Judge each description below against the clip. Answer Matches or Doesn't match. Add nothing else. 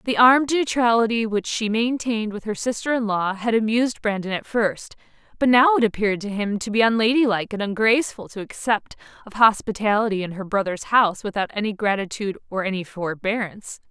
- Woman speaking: Matches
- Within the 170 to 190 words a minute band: Matches